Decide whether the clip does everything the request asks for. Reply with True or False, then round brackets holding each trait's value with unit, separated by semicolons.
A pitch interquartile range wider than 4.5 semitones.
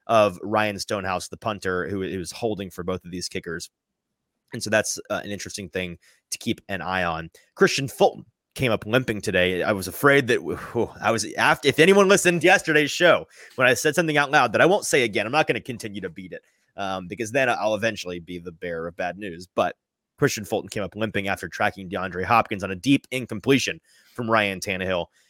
True (5.3 semitones)